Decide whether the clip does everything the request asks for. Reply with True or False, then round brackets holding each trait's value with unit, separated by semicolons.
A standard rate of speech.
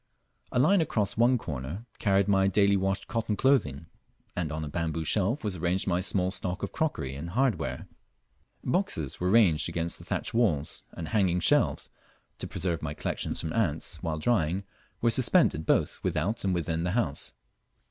True (170 wpm)